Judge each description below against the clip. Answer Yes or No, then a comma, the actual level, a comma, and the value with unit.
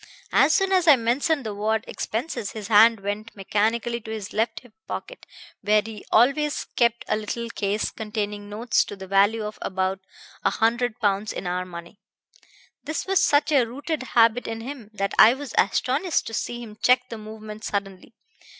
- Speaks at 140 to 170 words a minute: No, average, 180 wpm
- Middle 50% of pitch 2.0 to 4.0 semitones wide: Yes, average, 3.1 semitones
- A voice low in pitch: No, high, 220 Hz